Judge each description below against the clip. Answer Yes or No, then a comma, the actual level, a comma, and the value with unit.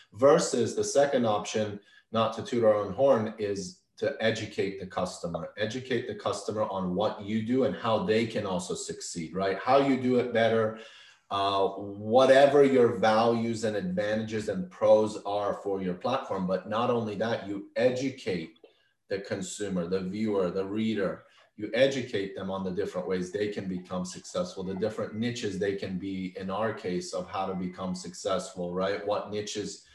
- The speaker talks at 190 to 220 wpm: No, average, 170 wpm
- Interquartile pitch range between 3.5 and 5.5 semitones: No, average, 3.0 semitones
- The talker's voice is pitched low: Yes, low, 105 Hz